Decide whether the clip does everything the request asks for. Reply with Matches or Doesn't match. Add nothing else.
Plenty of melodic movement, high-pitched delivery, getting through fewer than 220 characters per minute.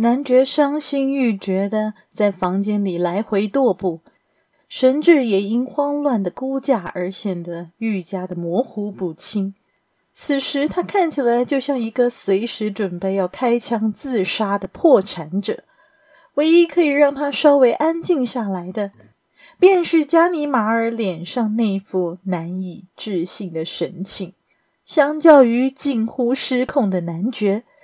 Matches